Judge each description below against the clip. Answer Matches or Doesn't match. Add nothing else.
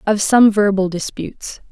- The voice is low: Doesn't match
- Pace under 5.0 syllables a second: Matches